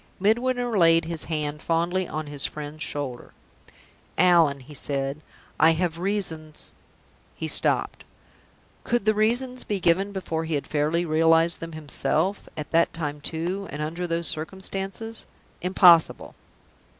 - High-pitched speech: No, medium, 165 Hz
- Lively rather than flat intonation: No, average, 3.7 semitones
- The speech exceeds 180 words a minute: No, average, 140 wpm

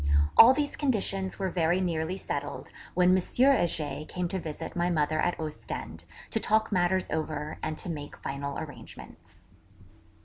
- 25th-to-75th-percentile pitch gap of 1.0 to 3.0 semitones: No, average, 3.4 semitones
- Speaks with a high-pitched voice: No, medium, 175 Hz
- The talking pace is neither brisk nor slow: Yes, average, 150 wpm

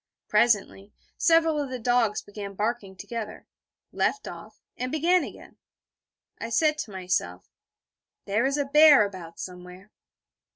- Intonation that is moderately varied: No, wide, 6.1 semitones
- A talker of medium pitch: No, high, 225 Hz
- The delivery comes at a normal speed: No, slow, 130 wpm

